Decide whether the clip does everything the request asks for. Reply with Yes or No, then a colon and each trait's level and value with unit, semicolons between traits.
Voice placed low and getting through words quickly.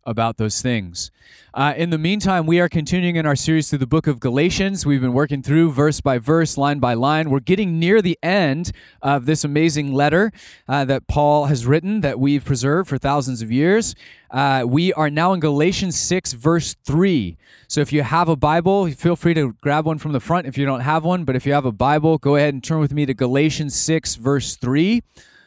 No: medium, 150 Hz; fast, 220 wpm